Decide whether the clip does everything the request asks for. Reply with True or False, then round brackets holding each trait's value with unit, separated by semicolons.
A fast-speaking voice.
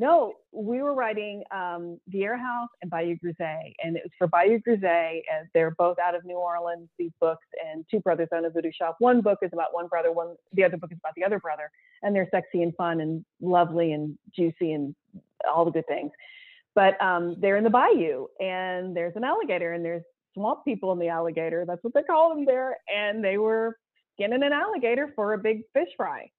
True (220 wpm)